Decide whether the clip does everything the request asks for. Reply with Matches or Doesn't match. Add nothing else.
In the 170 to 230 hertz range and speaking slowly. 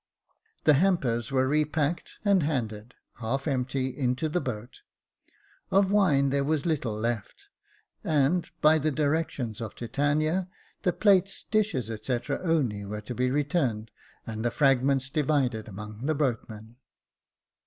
Doesn't match